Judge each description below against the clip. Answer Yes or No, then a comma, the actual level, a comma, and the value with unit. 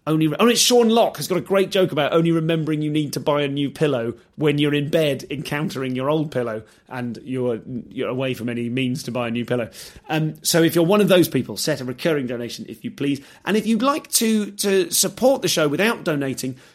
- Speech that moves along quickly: Yes, fast, 240 wpm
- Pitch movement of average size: No, wide, 5.8 semitones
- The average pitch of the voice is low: No, medium, 150 Hz